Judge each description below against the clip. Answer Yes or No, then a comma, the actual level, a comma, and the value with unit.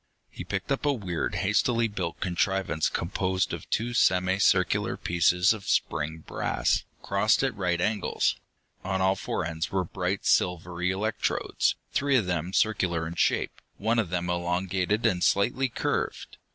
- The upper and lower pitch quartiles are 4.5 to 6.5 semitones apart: No, average, 3.2 semitones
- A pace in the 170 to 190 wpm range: No, average, 150 wpm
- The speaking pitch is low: Yes, very low, 95 Hz